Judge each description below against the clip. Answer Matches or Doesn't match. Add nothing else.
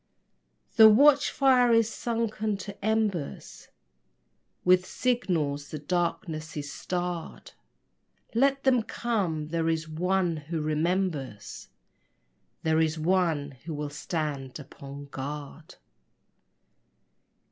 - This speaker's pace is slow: Matches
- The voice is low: Doesn't match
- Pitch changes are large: Matches